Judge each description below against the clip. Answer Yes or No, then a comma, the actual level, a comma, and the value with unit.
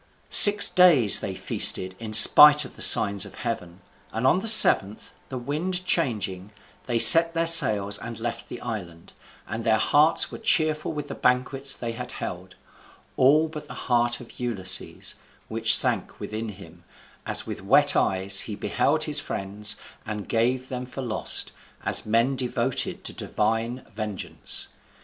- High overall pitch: No, low, 120 Hz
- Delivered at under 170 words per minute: Yes, average, 160 wpm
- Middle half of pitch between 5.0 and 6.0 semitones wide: Yes, average, 5.3 semitones